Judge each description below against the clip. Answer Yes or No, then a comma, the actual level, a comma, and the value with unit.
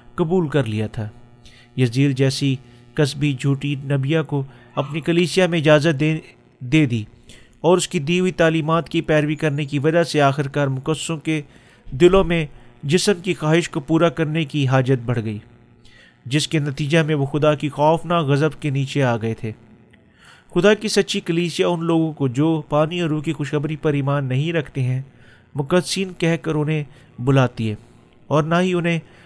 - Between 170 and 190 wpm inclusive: Yes, average, 175 wpm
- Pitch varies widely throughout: No, average, 3.9 semitones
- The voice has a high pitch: No, medium, 150 Hz